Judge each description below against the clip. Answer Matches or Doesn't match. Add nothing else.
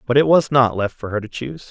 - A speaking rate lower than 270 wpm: Doesn't match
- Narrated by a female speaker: Doesn't match